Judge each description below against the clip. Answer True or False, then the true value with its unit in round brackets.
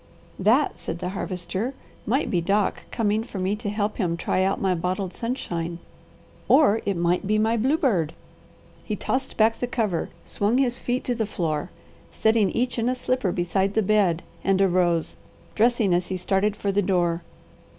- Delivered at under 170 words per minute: False (175 wpm)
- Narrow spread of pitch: False (4.1 semitones)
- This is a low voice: False (200 Hz)